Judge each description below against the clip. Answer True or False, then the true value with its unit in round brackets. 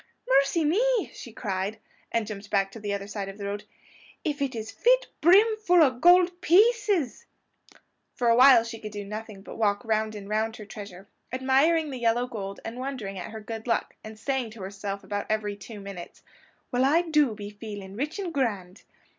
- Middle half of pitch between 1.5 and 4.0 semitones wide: False (5.3 semitones)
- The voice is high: True (225 Hz)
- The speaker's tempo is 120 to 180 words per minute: False (195 wpm)